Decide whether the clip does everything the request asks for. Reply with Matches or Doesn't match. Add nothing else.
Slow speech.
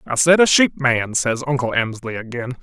Doesn't match